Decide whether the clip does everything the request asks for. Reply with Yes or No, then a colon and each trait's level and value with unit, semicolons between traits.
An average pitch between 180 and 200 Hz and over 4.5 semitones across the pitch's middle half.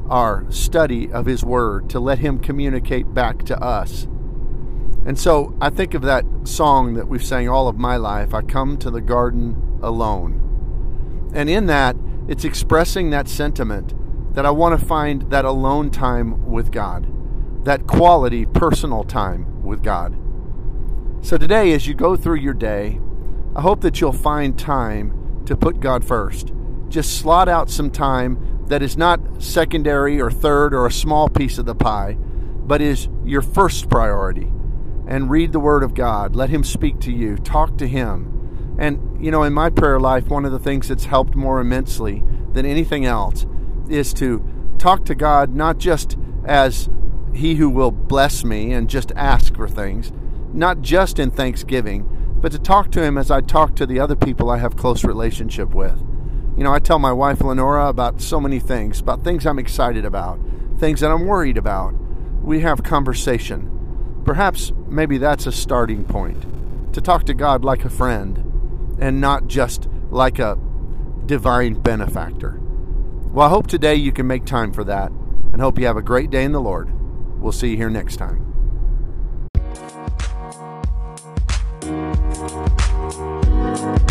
No: low, 125 Hz; average, 5.2 semitones